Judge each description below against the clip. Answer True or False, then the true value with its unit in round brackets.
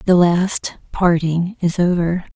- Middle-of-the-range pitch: True (175 Hz)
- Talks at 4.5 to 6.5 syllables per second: False (3.4 syllables/s)